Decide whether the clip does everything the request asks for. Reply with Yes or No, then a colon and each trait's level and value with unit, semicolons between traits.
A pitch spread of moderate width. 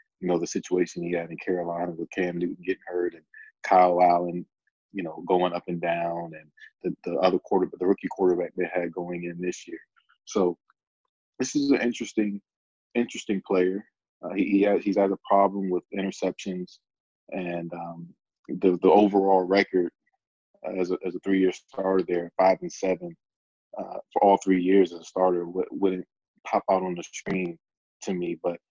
No: narrow, 2.1 semitones